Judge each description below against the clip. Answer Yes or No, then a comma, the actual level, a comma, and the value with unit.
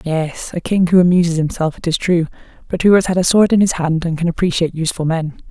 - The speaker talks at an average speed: No, fast, 250 wpm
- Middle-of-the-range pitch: Yes, medium, 170 Hz